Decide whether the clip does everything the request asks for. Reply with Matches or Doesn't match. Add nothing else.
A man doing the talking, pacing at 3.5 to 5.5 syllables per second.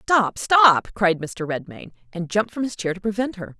Doesn't match